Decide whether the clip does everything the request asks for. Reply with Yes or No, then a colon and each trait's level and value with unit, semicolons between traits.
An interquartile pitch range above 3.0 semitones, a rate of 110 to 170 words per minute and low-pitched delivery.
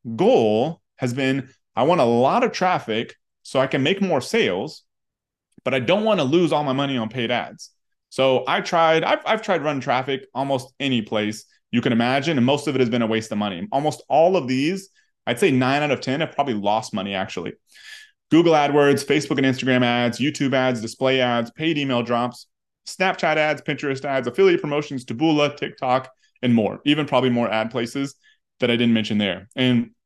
No: average, 3.9 semitones; average, 200 wpm; low, 130 Hz